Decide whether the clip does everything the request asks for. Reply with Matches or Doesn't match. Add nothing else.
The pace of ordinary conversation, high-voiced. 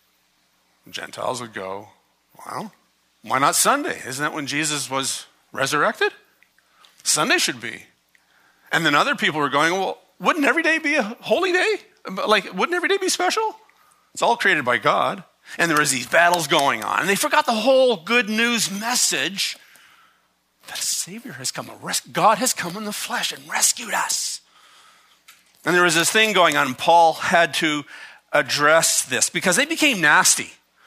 Matches